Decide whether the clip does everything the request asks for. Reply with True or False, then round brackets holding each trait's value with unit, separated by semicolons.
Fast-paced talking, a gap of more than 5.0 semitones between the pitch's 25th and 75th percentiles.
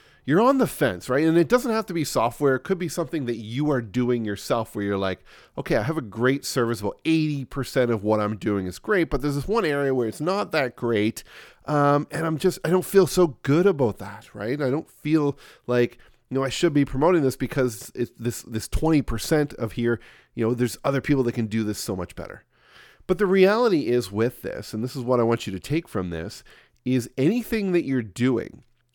True (230 wpm; 5.4 semitones)